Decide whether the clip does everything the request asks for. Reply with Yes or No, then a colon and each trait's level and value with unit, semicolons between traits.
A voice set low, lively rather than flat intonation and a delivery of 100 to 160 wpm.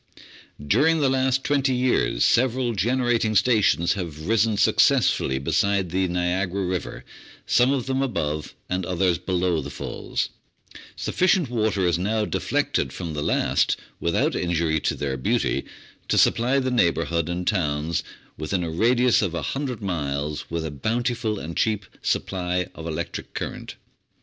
Yes: very low, 95 Hz; wide, 6.3 semitones; average, 145 wpm